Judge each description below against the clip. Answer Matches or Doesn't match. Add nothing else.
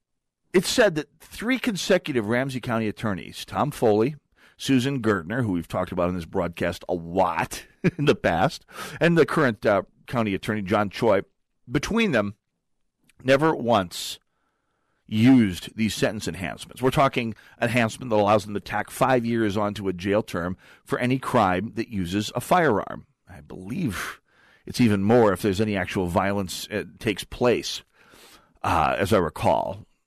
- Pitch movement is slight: Doesn't match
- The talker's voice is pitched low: Matches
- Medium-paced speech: Matches